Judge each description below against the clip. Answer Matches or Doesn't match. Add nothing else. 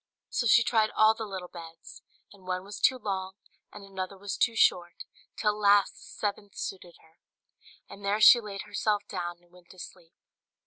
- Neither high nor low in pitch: Doesn't match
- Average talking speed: Matches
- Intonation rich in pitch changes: Doesn't match